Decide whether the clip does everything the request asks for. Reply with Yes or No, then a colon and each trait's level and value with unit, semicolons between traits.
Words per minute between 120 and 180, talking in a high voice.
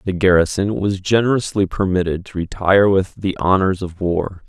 No: average, 160 wpm; very low, 95 Hz